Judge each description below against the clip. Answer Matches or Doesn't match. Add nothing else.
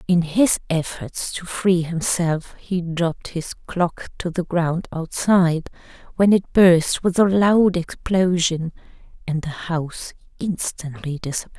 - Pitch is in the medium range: Matches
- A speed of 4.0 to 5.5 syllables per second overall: Matches